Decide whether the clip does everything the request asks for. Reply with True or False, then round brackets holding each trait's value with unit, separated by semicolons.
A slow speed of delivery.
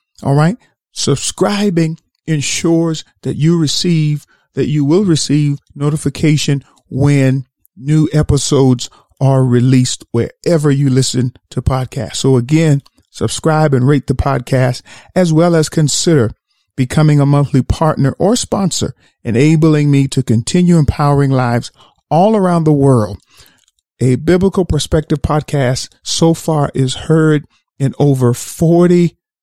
True (120 wpm)